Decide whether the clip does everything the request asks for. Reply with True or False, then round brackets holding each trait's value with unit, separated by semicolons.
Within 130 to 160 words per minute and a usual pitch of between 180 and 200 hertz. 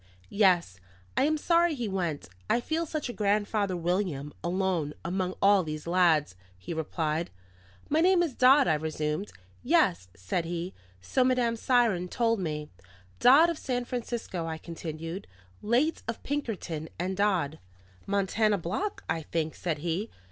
True (150 wpm; 185 Hz)